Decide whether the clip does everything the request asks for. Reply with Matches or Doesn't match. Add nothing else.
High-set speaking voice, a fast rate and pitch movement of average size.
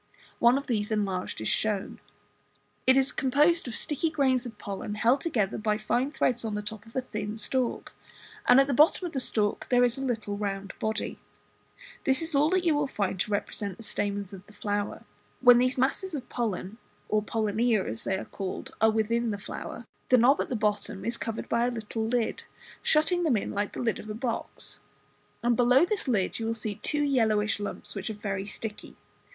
Matches